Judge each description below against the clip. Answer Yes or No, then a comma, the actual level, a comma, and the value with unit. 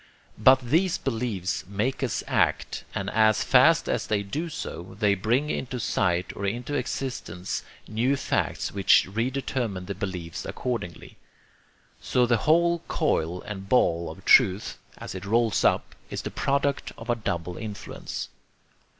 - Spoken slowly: No, average, 150 wpm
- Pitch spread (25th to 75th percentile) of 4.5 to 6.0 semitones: Yes, average, 5.3 semitones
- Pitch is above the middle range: No, low, 110 Hz